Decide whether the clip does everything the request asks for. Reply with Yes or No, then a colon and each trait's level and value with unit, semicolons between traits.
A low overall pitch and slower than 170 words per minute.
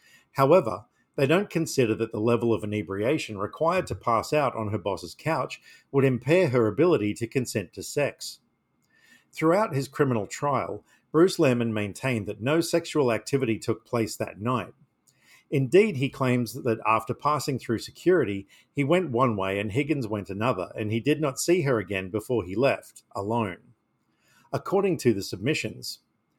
Yes: low, 120 Hz; average, 160 wpm